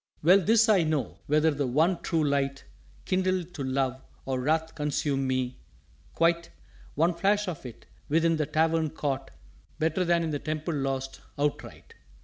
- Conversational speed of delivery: Yes, average, 155 wpm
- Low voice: No, medium, 155 Hz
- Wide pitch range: No, average, 3.5 semitones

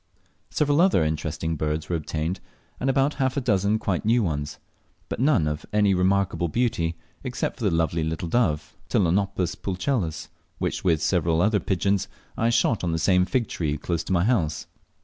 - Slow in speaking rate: No, average, 170 wpm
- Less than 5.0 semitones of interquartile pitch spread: No, average, 5.3 semitones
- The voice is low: Yes, very low, 90 Hz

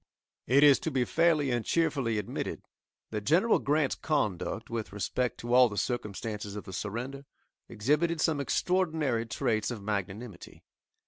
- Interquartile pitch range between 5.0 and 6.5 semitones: Yes, wide, 5.6 semitones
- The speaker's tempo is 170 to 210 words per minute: No, average, 145 wpm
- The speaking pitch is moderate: No, low, 120 Hz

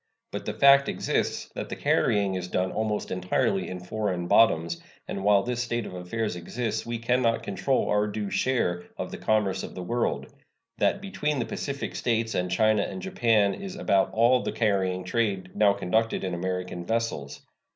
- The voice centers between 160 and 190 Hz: No, low, 105 Hz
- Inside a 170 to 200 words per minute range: Yes, average, 180 wpm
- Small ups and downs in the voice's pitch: No, average, 4.2 semitones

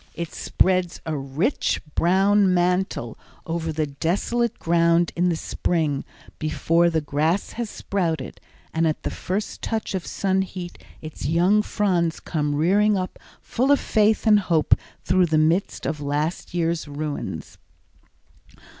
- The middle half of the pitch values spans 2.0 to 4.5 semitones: Yes, average, 3.4 semitones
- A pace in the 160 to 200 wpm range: No, average, 145 wpm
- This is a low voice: No, medium, 170 Hz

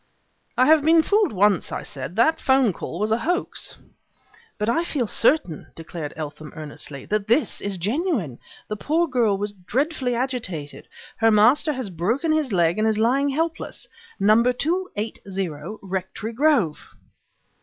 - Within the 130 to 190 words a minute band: Yes, average, 155 wpm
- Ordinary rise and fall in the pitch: No, wide, 7.2 semitones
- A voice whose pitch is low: No, high, 225 Hz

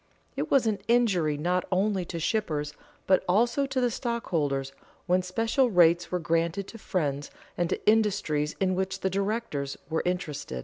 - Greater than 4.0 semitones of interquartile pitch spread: Yes, average, 5.0 semitones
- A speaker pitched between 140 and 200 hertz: Yes, medium, 185 Hz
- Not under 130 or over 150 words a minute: No, average, 165 wpm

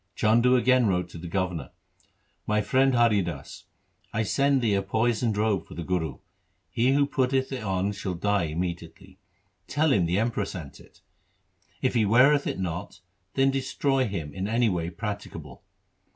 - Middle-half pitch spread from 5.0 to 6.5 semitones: Yes, wide, 5.6 semitones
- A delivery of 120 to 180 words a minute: Yes, average, 170 wpm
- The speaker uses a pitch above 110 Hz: No, low, 105 Hz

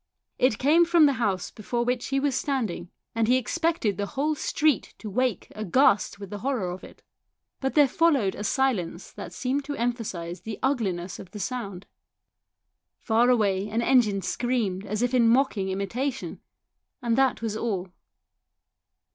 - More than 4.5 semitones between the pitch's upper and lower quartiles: Yes, average, 4.9 semitones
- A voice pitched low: No, high, 230 Hz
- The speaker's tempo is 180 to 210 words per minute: No, average, 165 wpm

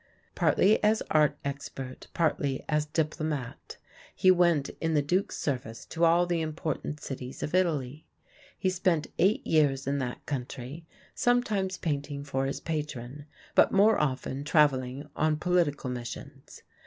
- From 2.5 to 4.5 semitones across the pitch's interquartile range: Yes, average, 3.8 semitones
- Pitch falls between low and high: Yes, medium, 150 Hz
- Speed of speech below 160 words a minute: Yes, average, 140 wpm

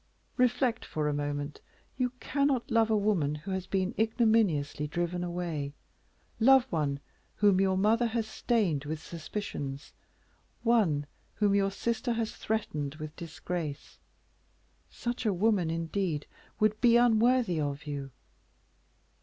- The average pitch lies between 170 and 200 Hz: Yes, high, 190 Hz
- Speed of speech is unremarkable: No, slow, 130 wpm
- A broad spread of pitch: Yes, wide, 6.9 semitones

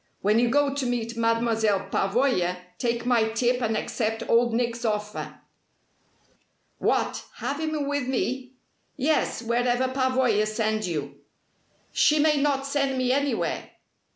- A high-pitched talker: Yes, high, 240 Hz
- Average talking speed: No, slow, 130 wpm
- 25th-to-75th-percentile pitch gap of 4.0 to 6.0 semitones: No, average, 3.2 semitones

